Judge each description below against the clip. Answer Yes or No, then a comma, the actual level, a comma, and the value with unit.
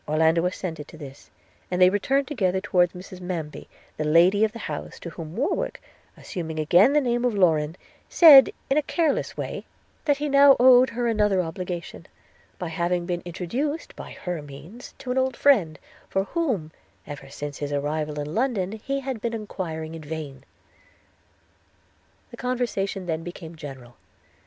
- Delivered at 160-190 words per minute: Yes, average, 165 wpm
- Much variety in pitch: Yes, wide, 7.4 semitones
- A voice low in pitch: No, medium, 180 Hz